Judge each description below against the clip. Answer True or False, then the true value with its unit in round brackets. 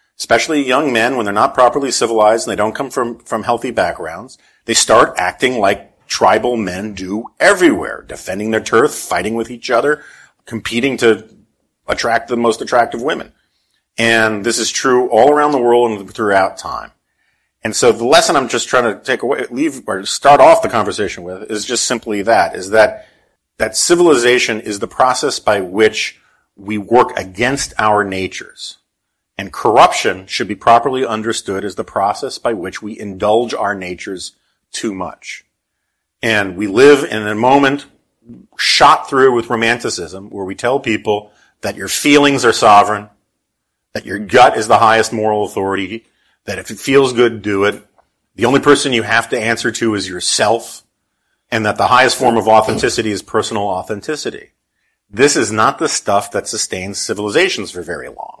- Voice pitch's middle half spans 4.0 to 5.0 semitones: False (2.7 semitones)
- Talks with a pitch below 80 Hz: False (110 Hz)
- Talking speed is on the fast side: False (170 wpm)